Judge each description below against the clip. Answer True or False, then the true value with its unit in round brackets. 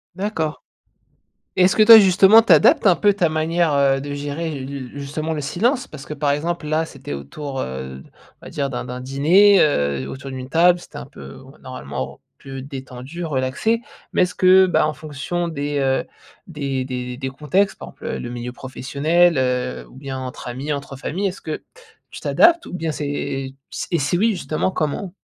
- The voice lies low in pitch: False (145 Hz)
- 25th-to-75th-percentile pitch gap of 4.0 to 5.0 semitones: True (4.7 semitones)